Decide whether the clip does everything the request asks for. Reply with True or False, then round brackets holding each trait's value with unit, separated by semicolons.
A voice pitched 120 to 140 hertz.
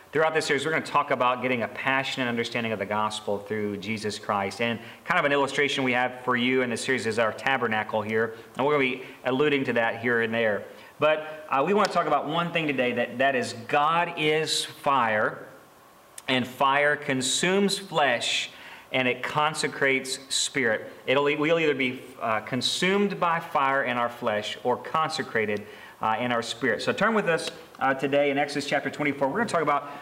True (135 Hz)